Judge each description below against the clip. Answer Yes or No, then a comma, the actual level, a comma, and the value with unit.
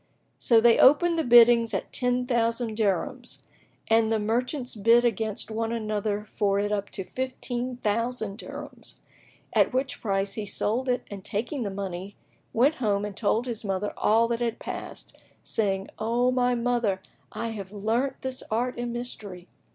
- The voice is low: No, high, 230 Hz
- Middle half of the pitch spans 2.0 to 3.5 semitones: Yes, average, 3.0 semitones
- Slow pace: No, average, 165 wpm